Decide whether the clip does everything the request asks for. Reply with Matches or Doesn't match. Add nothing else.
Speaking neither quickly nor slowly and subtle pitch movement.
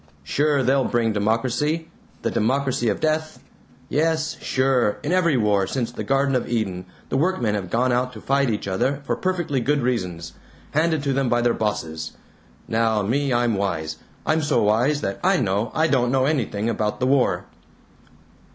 Doesn't match